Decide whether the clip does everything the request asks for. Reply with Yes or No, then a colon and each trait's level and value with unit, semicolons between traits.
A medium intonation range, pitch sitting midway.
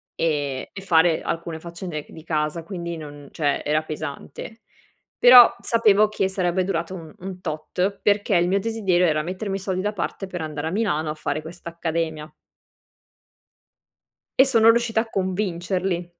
Yes: average, 3.7 semitones; medium, 175 Hz